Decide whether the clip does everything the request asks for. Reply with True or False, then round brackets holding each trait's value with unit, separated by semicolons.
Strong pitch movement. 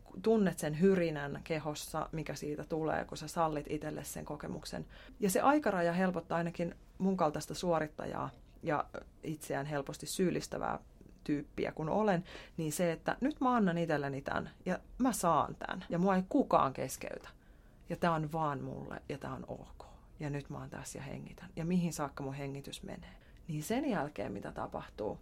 False (3.7 semitones)